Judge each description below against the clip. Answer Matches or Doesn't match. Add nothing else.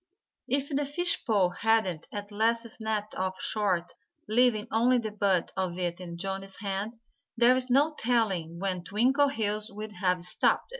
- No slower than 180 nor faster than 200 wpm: Doesn't match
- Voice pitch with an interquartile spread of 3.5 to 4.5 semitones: Matches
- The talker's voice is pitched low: Doesn't match